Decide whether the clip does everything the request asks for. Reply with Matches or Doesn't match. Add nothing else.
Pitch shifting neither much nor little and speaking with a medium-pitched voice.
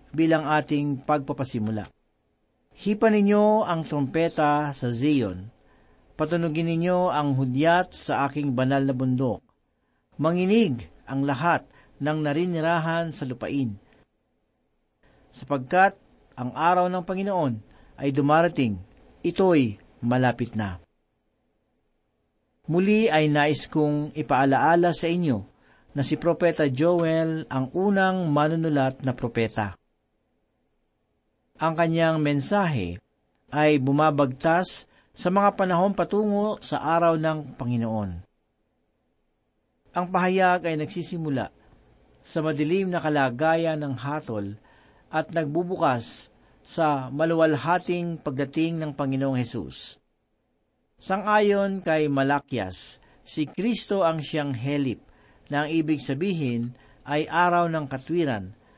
Matches